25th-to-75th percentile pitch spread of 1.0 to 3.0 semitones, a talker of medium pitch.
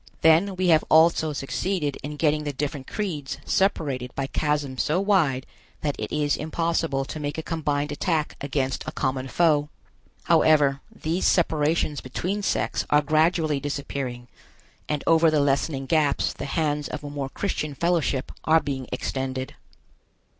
Yes: average, 2.7 semitones; medium, 150 Hz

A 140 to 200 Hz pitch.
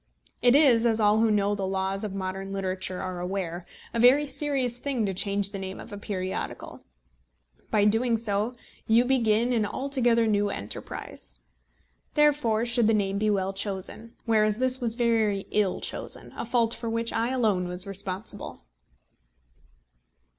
No: high, 215 Hz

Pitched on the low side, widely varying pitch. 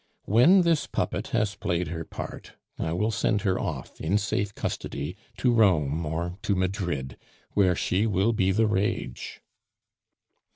No: very low, 95 Hz; average, 4.2 semitones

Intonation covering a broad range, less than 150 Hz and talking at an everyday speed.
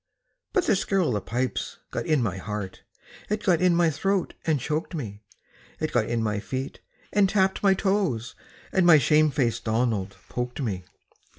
Yes: wide, 8.4 semitones; medium, 140 Hz; average, 180 wpm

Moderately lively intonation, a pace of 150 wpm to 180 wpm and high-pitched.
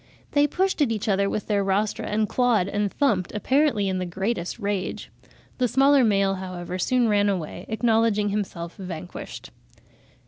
Yes: average, 3.5 semitones; average, 160 wpm; high, 205 Hz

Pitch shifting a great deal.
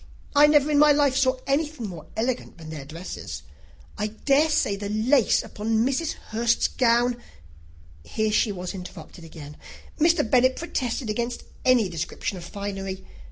Yes: wide, 6.3 semitones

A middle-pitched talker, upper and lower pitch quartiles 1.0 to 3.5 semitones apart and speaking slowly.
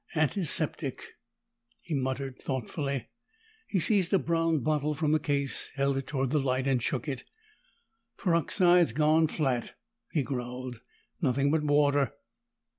Yes: medium, 145 Hz; average, 3.0 semitones; slow, 130 wpm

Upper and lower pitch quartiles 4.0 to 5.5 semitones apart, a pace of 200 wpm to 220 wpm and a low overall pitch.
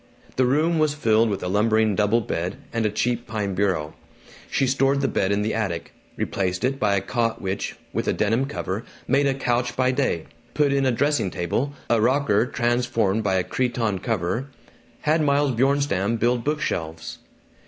No: average, 5.0 semitones; average, 185 wpm; low, 115 Hz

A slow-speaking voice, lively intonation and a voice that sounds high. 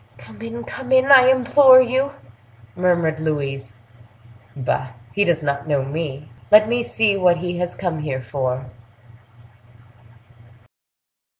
No: slow, 125 wpm; wide, 8.2 semitones; medium, 160 Hz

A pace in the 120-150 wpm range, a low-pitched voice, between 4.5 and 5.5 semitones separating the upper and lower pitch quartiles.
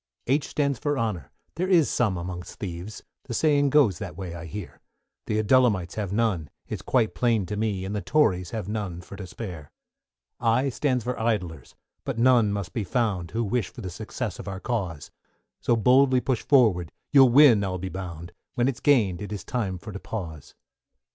No: average, 195 wpm; low, 105 Hz; average, 5.2 semitones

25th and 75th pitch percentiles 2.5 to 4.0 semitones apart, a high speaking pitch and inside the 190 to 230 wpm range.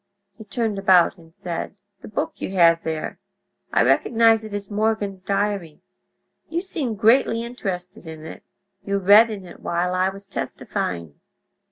No: average, 3.7 semitones; high, 195 Hz; average, 155 wpm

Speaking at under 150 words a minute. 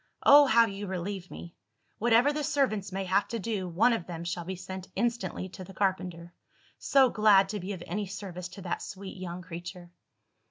No: average, 195 wpm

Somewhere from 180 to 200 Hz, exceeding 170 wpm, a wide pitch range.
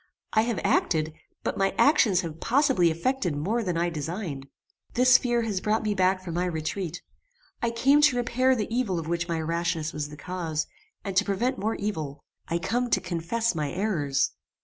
Yes: medium, 185 Hz; average, 190 wpm; wide, 5.8 semitones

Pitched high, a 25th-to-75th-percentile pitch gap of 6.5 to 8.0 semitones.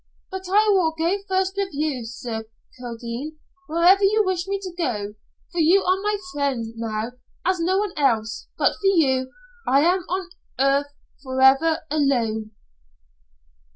Yes: very high, 310 Hz; wide, 6.8 semitones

